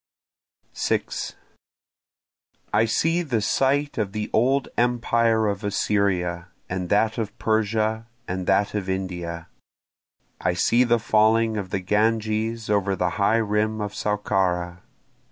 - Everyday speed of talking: No, slow, 125 wpm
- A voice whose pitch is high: No, low, 105 Hz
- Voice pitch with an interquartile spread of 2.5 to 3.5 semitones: Yes, average, 2.9 semitones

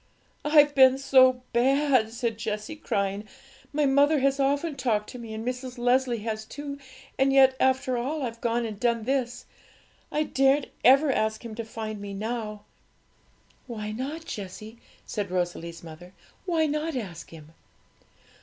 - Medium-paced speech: Yes, average, 155 wpm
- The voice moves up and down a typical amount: Yes, average, 4.0 semitones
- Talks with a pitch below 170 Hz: No, high, 245 Hz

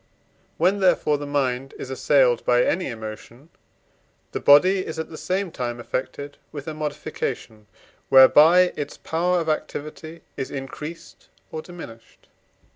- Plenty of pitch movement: No, average, 4.1 semitones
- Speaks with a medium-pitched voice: Yes, medium, 145 Hz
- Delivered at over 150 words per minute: No, slow, 135 wpm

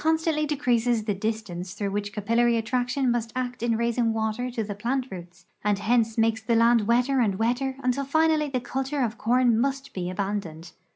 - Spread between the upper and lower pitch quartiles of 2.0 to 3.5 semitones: Yes, average, 3.2 semitones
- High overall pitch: Yes, high, 235 Hz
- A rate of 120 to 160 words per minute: No, average, 185 wpm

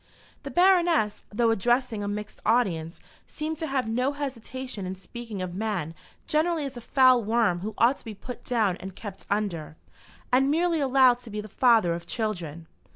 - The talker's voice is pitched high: Yes, high, 230 Hz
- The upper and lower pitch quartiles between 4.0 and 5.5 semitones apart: Yes, average, 4.7 semitones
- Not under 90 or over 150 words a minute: No, average, 180 wpm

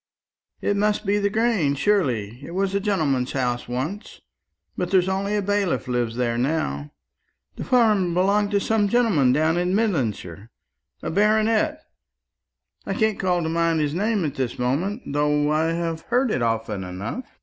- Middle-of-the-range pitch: Yes, medium, 170 Hz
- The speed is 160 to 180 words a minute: Yes, average, 165 wpm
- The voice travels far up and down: Yes, wide, 7.9 semitones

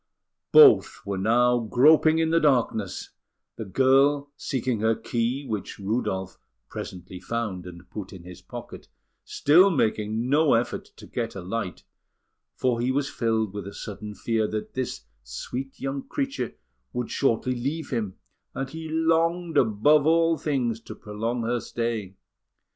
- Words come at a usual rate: Yes, average, 150 wpm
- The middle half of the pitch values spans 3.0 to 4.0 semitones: No, average, 5.2 semitones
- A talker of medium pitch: No, low, 120 Hz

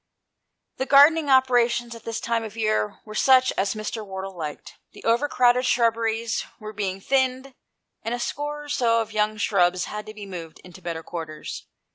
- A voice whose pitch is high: Yes, high, 225 Hz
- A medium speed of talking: Yes, average, 180 wpm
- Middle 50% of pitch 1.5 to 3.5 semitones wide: No, average, 4.0 semitones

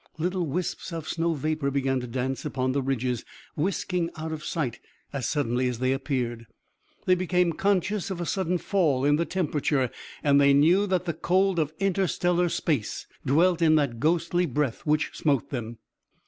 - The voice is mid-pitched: Yes, medium, 155 Hz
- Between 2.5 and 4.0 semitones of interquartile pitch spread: No, average, 4.8 semitones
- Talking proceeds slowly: No, average, 175 wpm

